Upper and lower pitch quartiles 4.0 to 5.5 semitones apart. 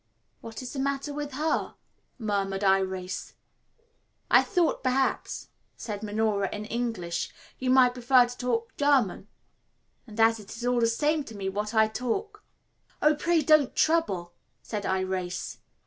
Yes: average, 5.2 semitones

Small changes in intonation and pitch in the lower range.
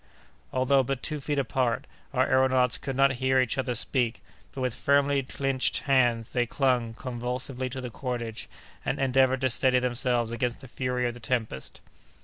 Yes: narrow, 1.6 semitones; low, 130 Hz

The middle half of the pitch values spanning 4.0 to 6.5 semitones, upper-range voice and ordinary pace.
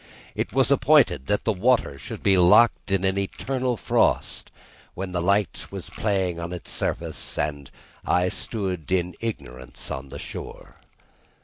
No: average, 4.3 semitones; very low, 95 Hz; average, 150 wpm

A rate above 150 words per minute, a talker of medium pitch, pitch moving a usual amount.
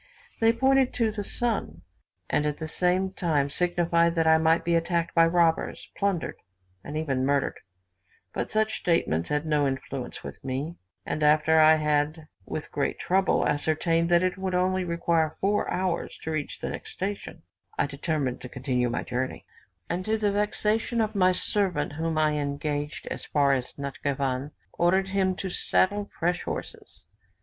Yes: average, 170 wpm; medium, 165 Hz; average, 4.2 semitones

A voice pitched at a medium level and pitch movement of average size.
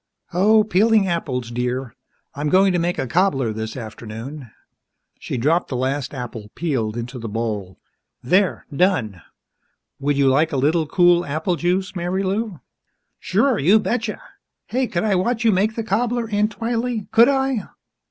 No: medium, 175 Hz; wide, 8.4 semitones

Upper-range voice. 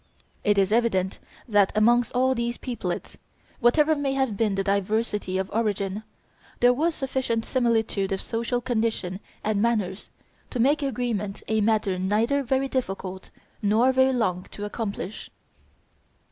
Yes: high, 225 Hz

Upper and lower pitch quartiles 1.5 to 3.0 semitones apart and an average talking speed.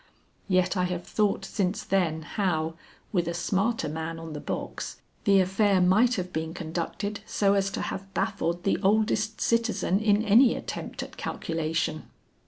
No: average, 3.7 semitones; average, 160 wpm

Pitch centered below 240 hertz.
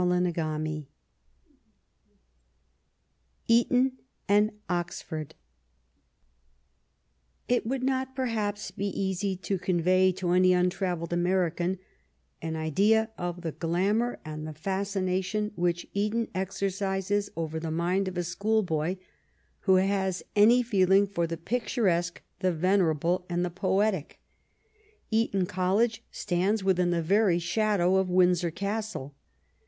Yes: medium, 185 Hz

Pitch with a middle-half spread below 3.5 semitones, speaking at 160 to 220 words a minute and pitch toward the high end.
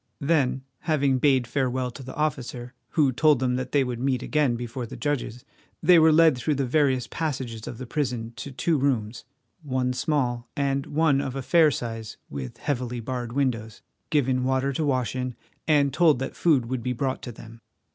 No: average, 2.8 semitones; average, 190 wpm; low, 130 Hz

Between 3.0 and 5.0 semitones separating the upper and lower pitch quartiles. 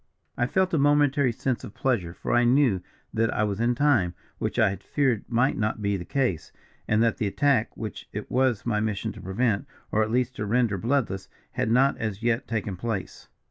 Yes: average, 3.7 semitones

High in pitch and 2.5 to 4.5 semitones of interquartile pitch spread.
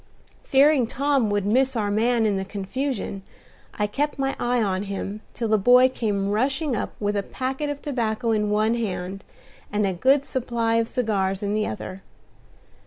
Yes: high, 225 Hz; average, 4.1 semitones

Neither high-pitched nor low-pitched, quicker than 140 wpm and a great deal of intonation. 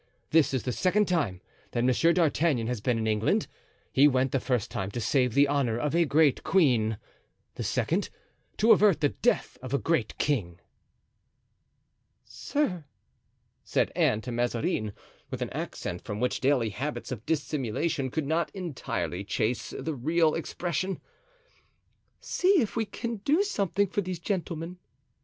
Yes: medium, 145 Hz; average, 155 wpm; wide, 6.1 semitones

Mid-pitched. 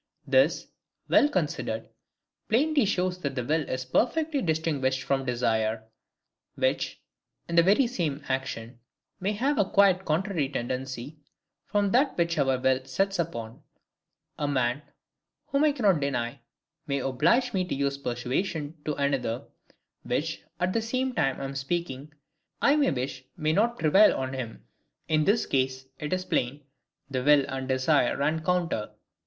Yes: medium, 150 Hz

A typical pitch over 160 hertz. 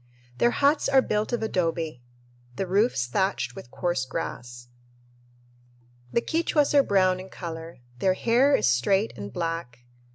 Yes: medium, 185 Hz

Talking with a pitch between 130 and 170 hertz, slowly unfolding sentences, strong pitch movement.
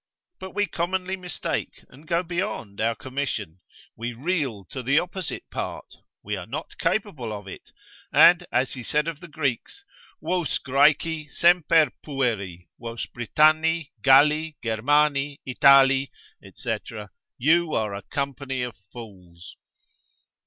Yes: medium, 140 Hz; slow, 130 wpm; wide, 5.7 semitones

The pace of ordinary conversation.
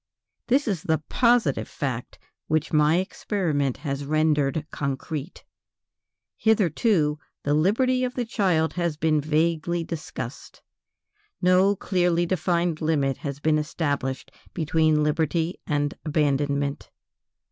No: slow, 110 wpm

